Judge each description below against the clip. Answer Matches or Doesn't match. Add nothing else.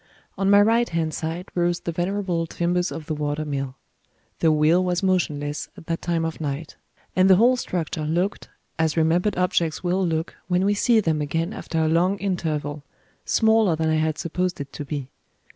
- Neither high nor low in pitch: Matches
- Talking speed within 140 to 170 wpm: Doesn't match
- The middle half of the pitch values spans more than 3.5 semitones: Doesn't match